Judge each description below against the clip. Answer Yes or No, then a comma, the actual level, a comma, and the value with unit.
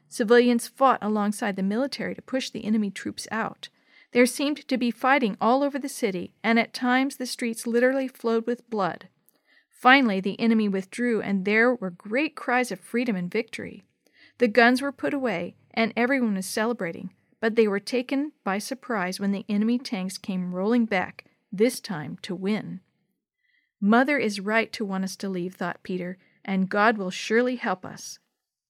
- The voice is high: Yes, high, 225 Hz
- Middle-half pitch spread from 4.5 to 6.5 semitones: No, average, 4.0 semitones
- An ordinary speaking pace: Yes, average, 175 wpm